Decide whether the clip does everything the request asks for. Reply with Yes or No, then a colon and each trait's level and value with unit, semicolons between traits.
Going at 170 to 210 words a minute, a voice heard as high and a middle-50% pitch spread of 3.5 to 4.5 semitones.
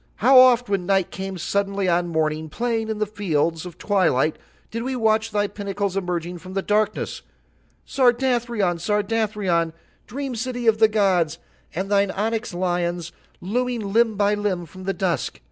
No: average, 160 wpm; high, 200 Hz; average, 3.9 semitones